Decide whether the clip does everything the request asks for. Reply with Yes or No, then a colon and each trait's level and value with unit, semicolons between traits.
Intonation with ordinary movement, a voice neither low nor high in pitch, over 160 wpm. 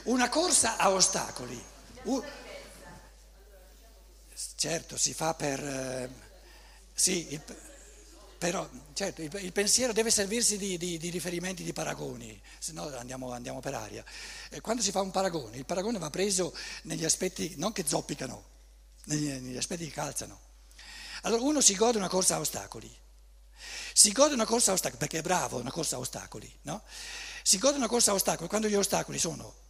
No: wide, 6.8 semitones; medium, 180 Hz; fast, 170 wpm